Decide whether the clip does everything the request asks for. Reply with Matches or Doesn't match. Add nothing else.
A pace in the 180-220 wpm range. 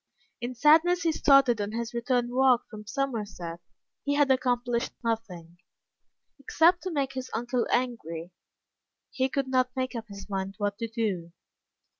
Doesn't match